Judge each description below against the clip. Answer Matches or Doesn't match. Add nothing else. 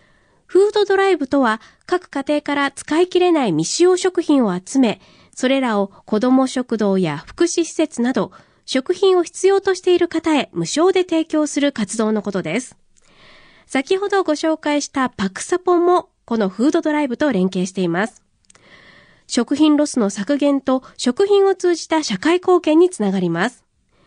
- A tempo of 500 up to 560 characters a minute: Doesn't match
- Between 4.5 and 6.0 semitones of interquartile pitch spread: Doesn't match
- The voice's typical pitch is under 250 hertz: Doesn't match